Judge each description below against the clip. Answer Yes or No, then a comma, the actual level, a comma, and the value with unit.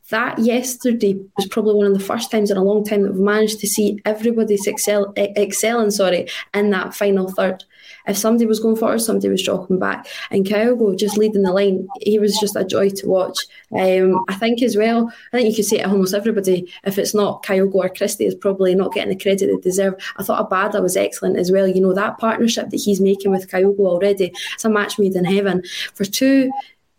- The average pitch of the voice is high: Yes, high, 205 Hz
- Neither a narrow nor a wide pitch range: No, narrow, 2.0 semitones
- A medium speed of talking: No, fast, 220 wpm